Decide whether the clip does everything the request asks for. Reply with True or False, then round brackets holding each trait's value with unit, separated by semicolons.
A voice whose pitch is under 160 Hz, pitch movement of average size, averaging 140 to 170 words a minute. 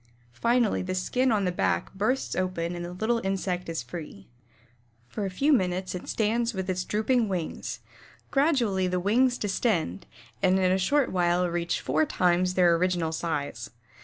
False (185 Hz; 3.9 semitones; 160 wpm)